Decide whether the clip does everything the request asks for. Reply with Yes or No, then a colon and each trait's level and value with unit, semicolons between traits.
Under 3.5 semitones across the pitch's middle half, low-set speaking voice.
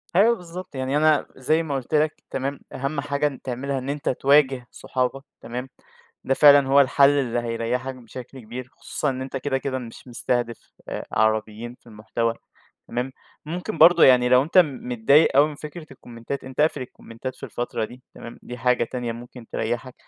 Yes: average, 2.7 semitones; low, 130 Hz